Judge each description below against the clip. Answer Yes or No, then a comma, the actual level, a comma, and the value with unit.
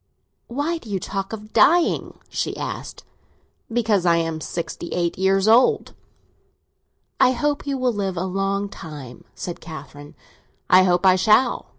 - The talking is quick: No, average, 155 wpm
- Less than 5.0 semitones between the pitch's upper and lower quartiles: No, average, 5.3 semitones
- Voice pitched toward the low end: No, high, 195 Hz